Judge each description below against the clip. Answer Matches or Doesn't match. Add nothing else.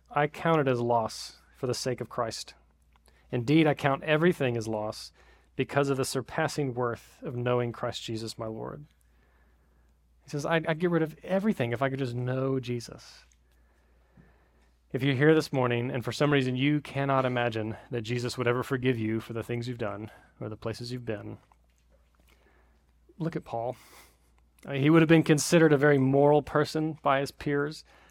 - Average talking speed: Matches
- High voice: Doesn't match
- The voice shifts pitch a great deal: Matches